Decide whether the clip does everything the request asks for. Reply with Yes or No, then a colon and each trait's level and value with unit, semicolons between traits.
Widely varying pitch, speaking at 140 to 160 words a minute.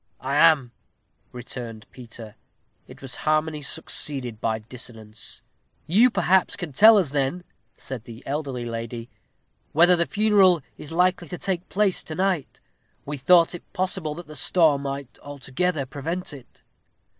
Yes: wide, 5.9 semitones; average, 145 wpm